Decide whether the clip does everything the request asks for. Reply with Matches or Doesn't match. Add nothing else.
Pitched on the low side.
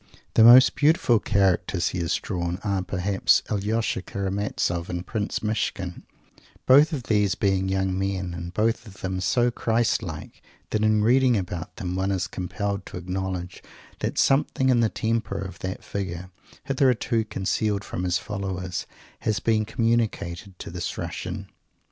Matches